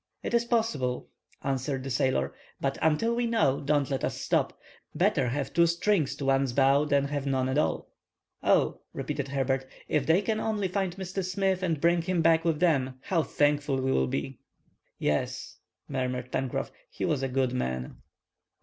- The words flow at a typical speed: Yes, average, 175 wpm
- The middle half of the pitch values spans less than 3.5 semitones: No, average, 4.8 semitones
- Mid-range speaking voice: Yes, medium, 145 Hz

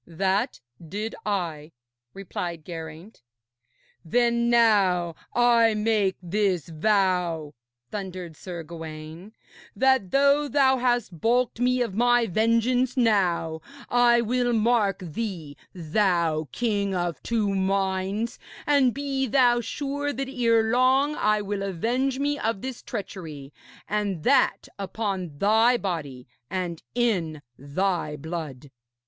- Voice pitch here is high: Yes, high, 205 Hz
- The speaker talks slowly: Yes, slow, 115 wpm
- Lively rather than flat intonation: Yes, wide, 5.7 semitones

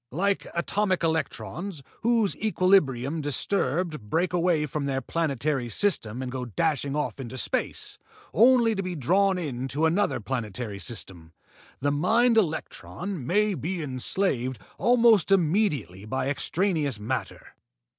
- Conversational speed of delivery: No, slow, 125 wpm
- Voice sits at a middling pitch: Yes, medium, 155 Hz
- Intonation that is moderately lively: No, wide, 6.9 semitones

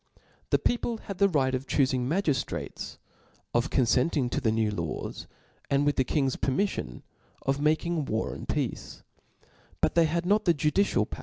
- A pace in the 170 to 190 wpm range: Yes, average, 175 wpm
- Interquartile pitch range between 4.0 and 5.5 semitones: Yes, average, 4.9 semitones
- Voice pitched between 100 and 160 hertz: Yes, medium, 140 Hz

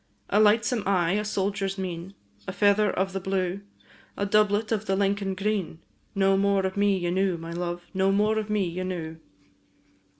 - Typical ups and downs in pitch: No, narrow, 1.8 semitones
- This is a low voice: No, high, 195 Hz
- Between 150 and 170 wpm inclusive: No, average, 180 wpm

